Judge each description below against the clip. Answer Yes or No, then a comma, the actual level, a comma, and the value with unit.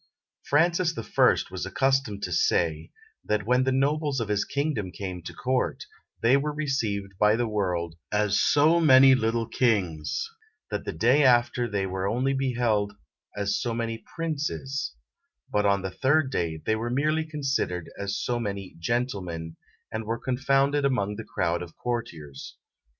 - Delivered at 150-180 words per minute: Yes, average, 160 wpm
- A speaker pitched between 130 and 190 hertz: No, low, 115 Hz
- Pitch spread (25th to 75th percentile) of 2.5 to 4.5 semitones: No, average, 5.3 semitones